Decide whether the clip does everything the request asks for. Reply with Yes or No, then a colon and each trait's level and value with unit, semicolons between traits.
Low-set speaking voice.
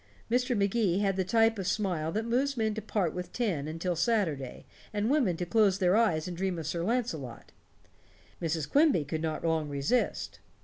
No: high, 190 Hz